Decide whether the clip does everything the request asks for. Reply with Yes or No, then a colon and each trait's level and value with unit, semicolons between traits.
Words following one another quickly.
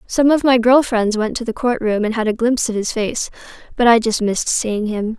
Yes: fast, 265 wpm